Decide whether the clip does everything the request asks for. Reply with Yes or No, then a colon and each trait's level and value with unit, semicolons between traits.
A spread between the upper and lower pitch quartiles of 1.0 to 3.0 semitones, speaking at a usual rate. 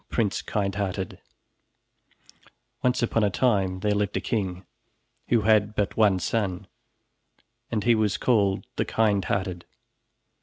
No: narrow, 2.4 semitones; slow, 120 wpm